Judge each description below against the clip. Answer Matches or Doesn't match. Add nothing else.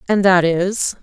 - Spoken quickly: Doesn't match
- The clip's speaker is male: Doesn't match